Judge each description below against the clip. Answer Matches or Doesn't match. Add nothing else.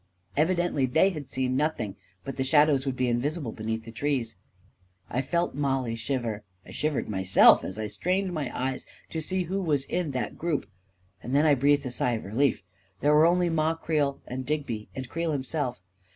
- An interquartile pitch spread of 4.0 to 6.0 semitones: Matches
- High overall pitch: Doesn't match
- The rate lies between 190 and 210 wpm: Matches